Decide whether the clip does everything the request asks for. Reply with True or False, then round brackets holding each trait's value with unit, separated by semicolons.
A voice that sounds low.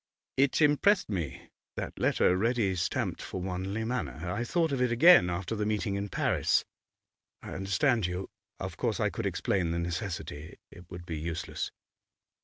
True (95 Hz)